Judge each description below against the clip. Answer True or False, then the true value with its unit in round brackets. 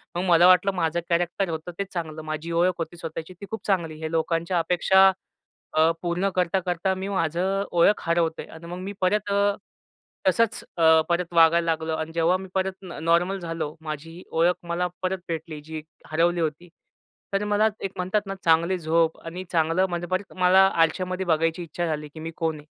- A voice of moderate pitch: True (170 Hz)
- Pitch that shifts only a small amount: True (2.2 semitones)